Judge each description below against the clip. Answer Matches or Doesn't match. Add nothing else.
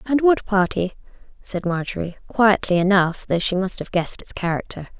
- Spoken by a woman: Matches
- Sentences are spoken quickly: Doesn't match